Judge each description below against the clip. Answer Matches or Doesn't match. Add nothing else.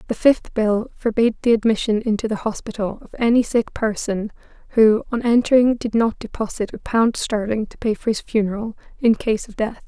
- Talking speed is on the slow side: Doesn't match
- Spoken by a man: Doesn't match